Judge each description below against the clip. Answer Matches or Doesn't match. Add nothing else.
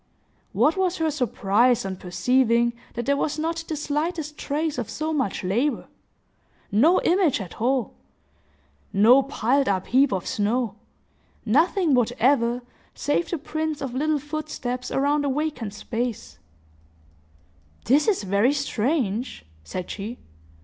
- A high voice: Matches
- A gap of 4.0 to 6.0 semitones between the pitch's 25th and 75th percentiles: Matches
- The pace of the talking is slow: Matches